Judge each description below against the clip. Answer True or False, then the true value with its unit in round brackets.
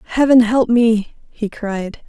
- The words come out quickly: False (145 wpm)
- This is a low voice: False (225 Hz)